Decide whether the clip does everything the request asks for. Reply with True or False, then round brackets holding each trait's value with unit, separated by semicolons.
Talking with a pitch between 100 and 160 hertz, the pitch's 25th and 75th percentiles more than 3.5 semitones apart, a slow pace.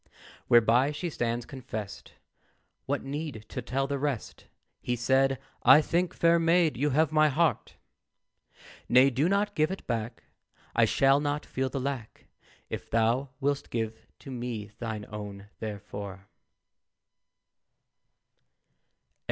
True (135 Hz; 4.4 semitones; 125 wpm)